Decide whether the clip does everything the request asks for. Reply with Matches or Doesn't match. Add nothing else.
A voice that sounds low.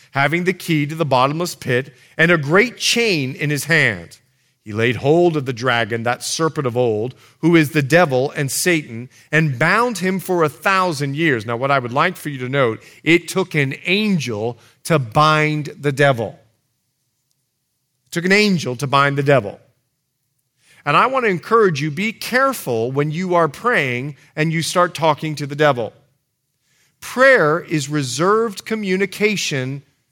Doesn't match